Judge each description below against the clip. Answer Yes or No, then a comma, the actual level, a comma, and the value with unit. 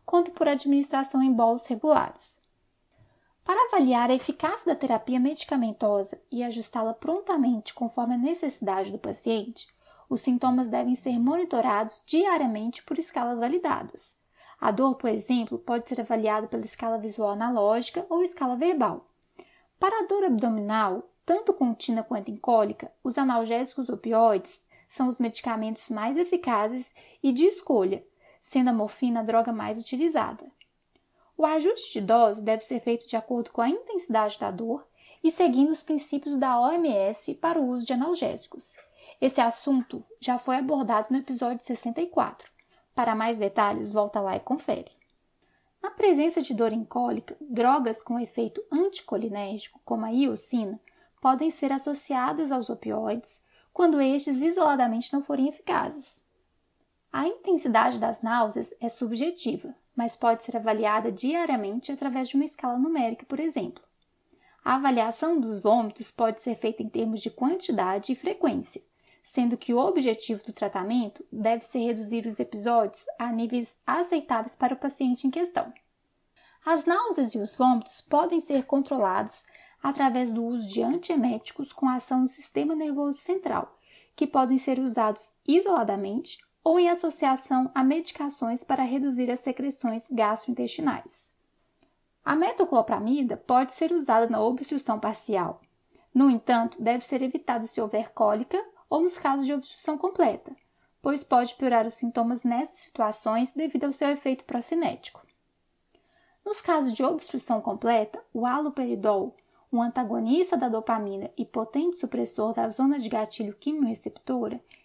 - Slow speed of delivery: No, average, 140 wpm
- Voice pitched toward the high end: Yes, very high, 255 Hz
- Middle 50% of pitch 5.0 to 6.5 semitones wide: Yes, average, 5.3 semitones